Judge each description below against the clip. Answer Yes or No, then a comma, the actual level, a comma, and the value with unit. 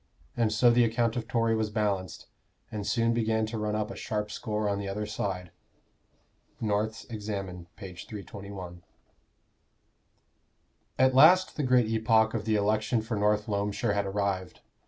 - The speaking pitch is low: Yes, low, 105 Hz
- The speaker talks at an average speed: Yes, average, 155 wpm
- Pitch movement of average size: No, narrow, 1.9 semitones